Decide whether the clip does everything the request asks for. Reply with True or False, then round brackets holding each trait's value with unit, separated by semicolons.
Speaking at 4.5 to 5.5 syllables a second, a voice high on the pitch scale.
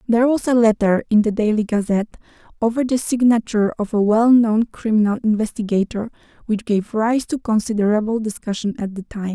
False (5.8 syllables/s; 220 Hz)